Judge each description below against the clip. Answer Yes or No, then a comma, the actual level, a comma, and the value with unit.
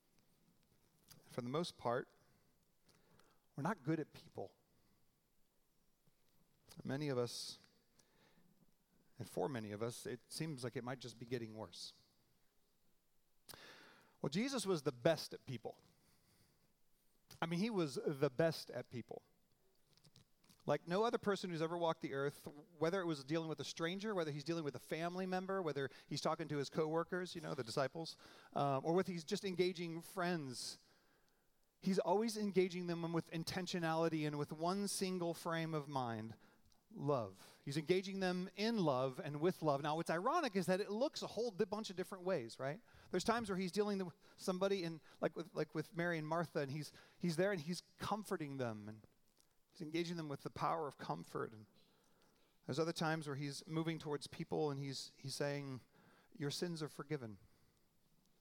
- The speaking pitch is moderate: Yes, medium, 165 Hz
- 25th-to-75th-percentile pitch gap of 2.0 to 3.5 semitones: No, average, 4.4 semitones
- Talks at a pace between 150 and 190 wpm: Yes, average, 175 wpm